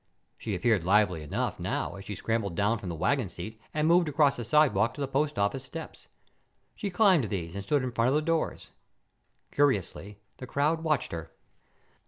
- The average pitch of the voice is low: Yes, low, 120 Hz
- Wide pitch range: Yes, wide, 7.0 semitones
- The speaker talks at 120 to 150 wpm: No, average, 190 wpm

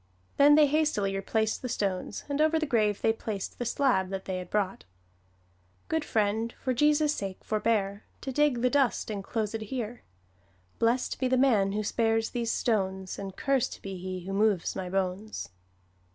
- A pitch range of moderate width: Yes, average, 4.8 semitones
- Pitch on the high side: Yes, high, 220 Hz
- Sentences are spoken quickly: No, average, 170 wpm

